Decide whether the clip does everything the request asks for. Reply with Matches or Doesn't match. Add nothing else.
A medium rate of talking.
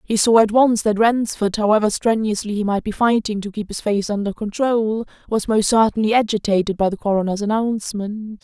Matches